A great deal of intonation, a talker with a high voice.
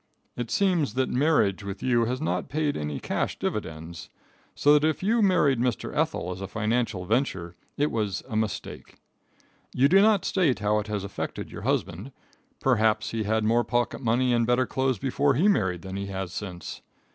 No: wide, 5.7 semitones; low, 115 Hz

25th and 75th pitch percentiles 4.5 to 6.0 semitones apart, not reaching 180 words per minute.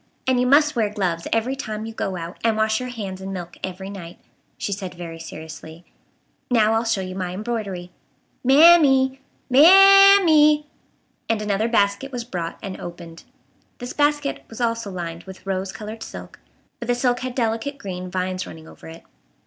No: wide, 5.4 semitones; average, 190 wpm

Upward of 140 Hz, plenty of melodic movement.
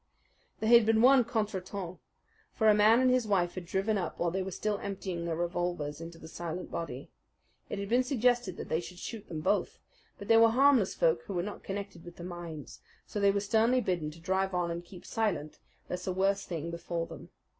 No: high, 190 Hz; average, 3.9 semitones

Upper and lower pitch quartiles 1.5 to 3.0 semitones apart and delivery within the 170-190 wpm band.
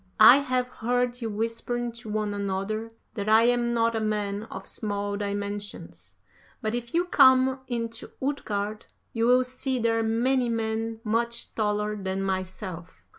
No: average, 2.7 semitones; average, 150 wpm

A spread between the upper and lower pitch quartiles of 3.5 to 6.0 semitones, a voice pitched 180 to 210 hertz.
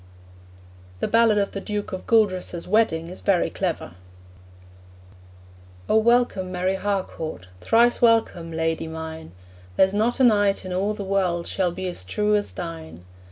Yes: average, 3.8 semitones; high, 190 Hz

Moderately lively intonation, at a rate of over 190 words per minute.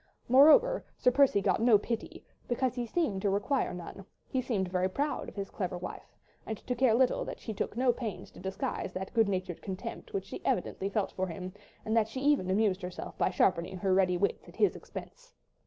Yes: average, 5.0 semitones; fast, 205 wpm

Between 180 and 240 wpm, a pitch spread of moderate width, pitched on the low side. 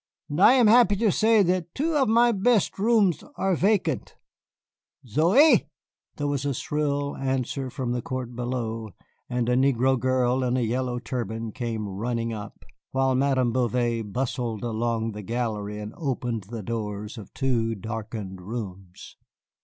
No: average, 155 wpm; average, 4.3 semitones; low, 125 Hz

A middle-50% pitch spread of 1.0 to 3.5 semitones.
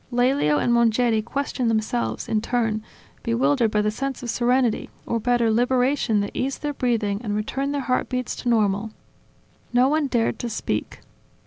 Yes: average, 2.8 semitones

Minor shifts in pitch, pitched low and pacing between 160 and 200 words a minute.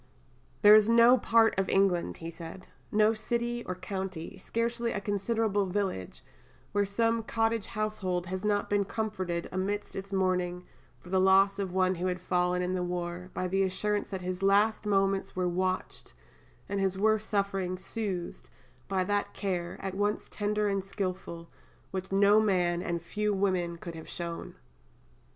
No: narrow, 2.3 semitones; high, 195 Hz; average, 165 wpm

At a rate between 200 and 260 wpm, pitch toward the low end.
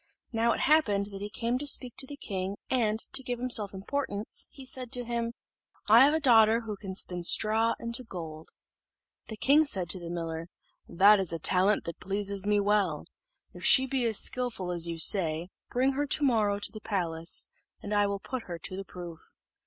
No: fast, 205 wpm; high, 210 Hz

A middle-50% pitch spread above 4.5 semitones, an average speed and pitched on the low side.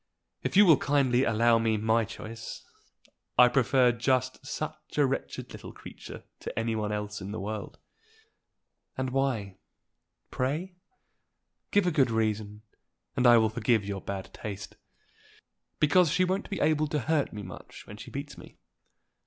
Yes: average, 4.9 semitones; average, 155 wpm; low, 120 Hz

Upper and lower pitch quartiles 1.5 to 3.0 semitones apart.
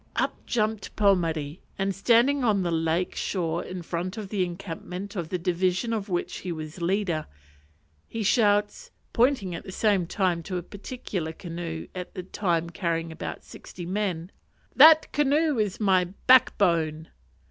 No: average, 3.7 semitones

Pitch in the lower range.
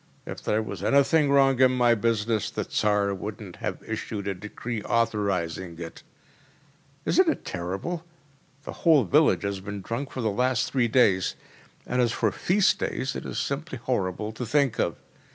Yes: low, 115 Hz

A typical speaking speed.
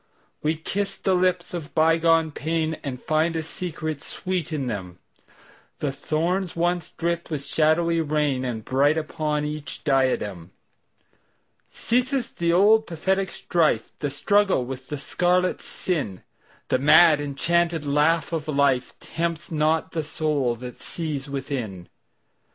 No: slow, 115 wpm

